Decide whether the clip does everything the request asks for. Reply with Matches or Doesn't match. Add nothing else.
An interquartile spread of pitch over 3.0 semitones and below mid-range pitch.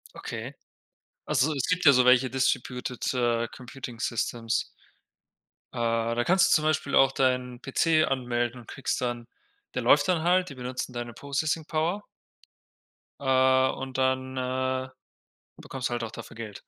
Doesn't match